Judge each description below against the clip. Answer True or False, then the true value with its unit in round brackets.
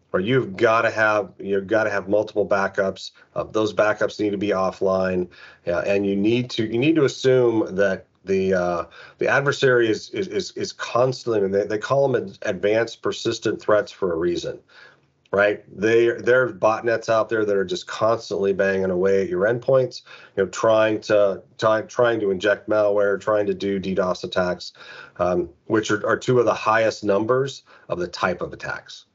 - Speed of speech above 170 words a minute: True (185 wpm)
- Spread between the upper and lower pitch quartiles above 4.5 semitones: False (2.8 semitones)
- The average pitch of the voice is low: True (105 Hz)